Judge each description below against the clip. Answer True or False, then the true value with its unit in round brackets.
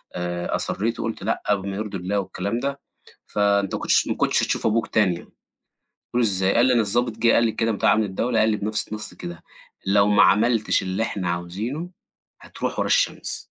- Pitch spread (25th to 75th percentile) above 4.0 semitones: False (3.0 semitones)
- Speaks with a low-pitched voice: True (105 Hz)